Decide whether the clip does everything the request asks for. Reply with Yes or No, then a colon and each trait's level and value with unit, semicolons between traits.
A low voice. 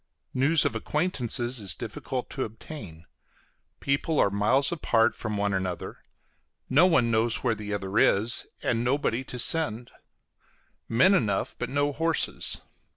Yes: low, 120 Hz